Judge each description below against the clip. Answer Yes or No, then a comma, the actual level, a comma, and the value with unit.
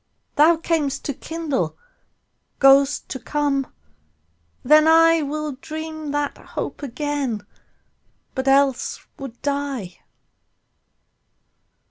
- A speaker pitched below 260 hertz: No, very high, 285 Hz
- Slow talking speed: Yes, slow, 85 wpm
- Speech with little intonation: Yes, narrow, 2.2 semitones